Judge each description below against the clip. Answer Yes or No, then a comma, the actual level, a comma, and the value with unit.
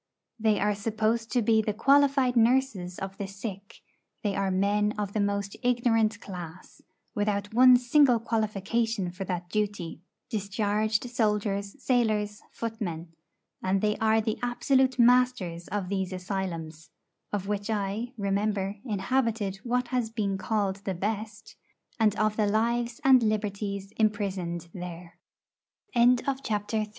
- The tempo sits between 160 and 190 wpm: No, average, 140 wpm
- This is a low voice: No, high, 210 Hz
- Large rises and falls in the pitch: No, average, 2.7 semitones